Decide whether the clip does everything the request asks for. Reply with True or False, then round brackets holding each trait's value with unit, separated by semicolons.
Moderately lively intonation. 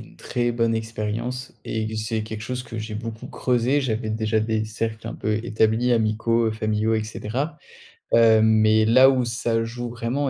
False (1.6 semitones)